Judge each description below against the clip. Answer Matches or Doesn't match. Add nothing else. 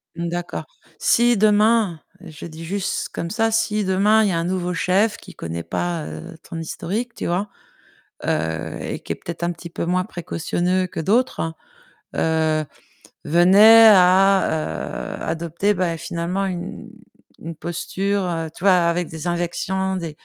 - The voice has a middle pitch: Matches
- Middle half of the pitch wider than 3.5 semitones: Doesn't match